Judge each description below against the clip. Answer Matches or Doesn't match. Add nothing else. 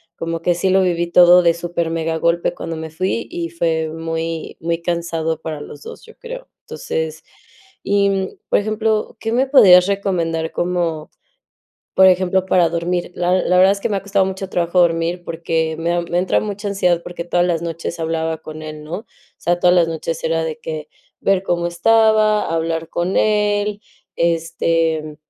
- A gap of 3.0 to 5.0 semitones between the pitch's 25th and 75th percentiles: Doesn't match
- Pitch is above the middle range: Doesn't match